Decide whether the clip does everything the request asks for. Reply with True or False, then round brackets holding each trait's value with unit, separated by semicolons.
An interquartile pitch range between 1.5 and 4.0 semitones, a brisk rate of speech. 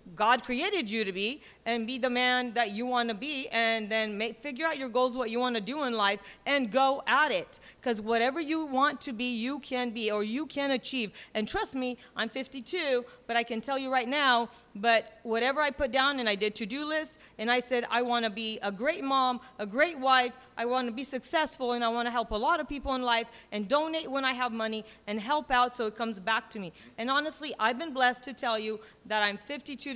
True (3.3 semitones; 245 wpm)